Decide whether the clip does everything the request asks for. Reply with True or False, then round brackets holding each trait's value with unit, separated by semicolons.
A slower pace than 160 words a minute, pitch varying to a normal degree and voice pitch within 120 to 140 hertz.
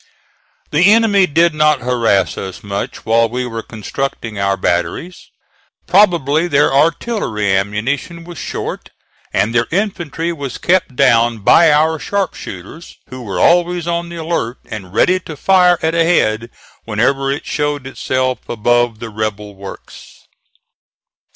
False (140 wpm; 7.4 semitones; 135 Hz)